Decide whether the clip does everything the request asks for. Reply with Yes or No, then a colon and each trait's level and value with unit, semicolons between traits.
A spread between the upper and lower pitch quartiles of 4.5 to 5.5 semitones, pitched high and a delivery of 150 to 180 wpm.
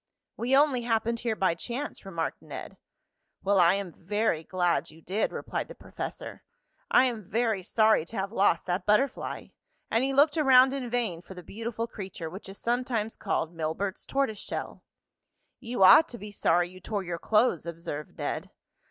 Yes: average, 5.1 semitones; high, 210 Hz; average, 175 wpm